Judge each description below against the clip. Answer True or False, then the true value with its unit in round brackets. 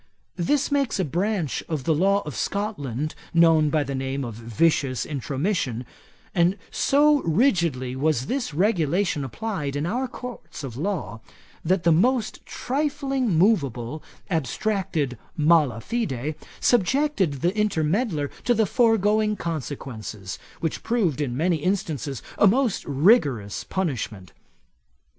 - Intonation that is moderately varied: False (7.3 semitones)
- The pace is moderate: False (125 wpm)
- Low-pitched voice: False (165 Hz)